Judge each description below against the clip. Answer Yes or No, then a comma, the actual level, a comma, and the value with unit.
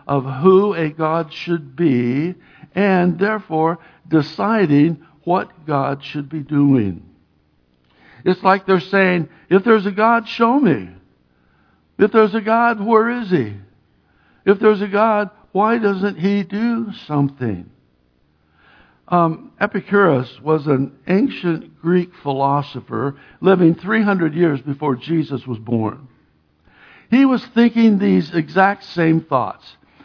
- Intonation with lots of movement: Yes, wide, 6.7 semitones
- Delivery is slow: Yes, slow, 120 wpm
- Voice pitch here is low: No, medium, 165 Hz